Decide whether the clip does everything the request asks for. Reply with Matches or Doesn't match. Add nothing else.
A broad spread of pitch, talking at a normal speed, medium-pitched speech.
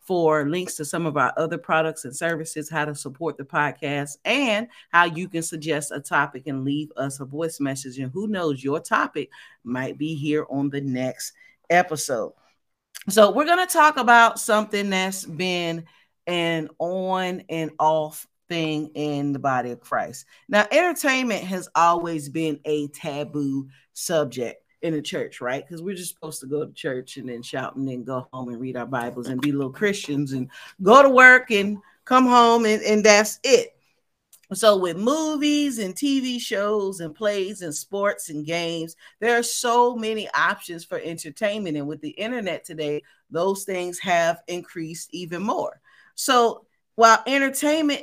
Matches